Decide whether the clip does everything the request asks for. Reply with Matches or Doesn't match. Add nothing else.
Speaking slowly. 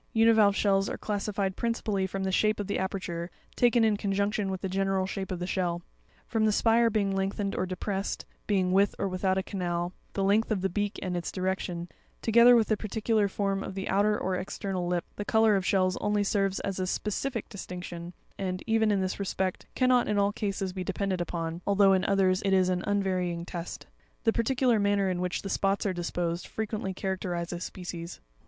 Doesn't match